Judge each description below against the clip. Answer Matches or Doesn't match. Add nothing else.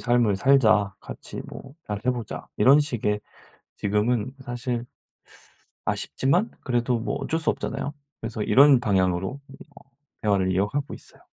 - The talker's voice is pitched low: Matches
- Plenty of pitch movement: Doesn't match